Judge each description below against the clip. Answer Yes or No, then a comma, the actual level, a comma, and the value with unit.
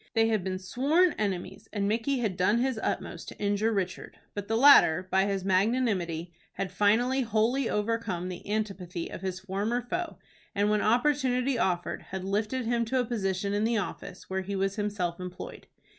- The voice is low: No, high, 205 Hz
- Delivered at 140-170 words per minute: No, average, 180 wpm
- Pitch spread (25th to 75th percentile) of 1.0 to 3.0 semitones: No, average, 3.8 semitones